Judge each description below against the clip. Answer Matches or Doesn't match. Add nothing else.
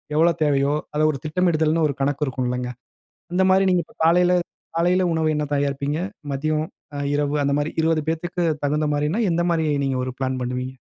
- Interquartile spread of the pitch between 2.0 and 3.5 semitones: Matches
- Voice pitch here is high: Doesn't match